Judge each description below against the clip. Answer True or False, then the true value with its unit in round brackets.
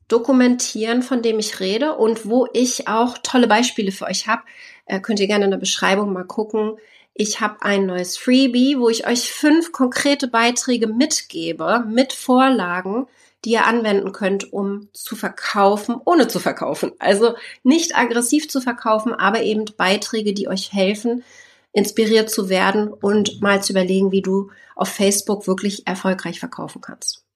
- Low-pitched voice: False (220 Hz)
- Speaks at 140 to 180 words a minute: True (160 wpm)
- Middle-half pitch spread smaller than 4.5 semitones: True (3.6 semitones)